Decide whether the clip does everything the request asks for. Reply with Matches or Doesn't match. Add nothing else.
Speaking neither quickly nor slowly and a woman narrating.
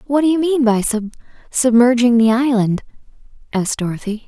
Matches